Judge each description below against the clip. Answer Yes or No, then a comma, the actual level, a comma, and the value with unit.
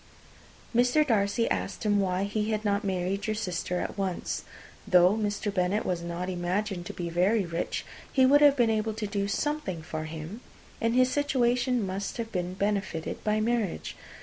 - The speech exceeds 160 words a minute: Yes, average, 175 wpm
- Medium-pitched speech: No, high, 205 Hz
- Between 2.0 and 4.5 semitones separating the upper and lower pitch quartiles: Yes, average, 3.9 semitones